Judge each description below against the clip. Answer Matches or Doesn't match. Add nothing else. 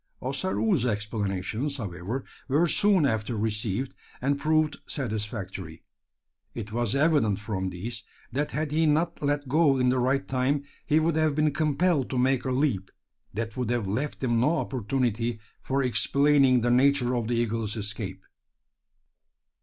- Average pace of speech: Matches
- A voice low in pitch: Matches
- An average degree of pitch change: Matches